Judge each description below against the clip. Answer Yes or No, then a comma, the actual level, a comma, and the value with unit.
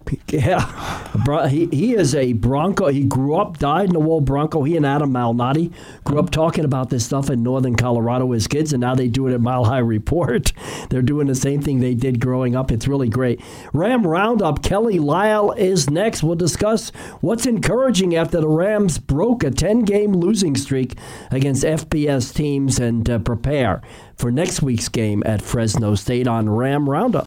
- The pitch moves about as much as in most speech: Yes, average, 4.6 semitones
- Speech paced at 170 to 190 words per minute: Yes, average, 185 wpm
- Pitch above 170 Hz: No, medium, 140 Hz